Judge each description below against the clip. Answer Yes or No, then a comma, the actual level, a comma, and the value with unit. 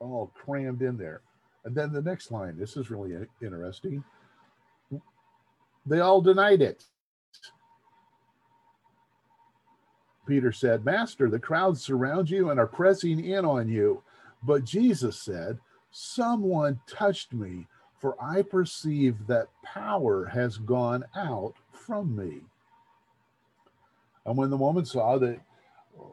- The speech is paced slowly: Yes, slow, 120 wpm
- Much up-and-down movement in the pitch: Yes, wide, 7.8 semitones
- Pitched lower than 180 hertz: Yes, medium, 140 Hz